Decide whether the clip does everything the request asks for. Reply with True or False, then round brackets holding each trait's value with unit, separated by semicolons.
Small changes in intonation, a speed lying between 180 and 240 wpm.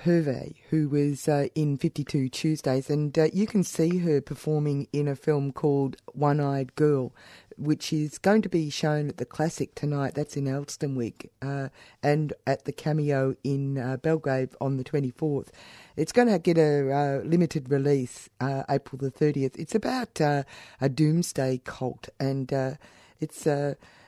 False (2.2 semitones; 165 wpm)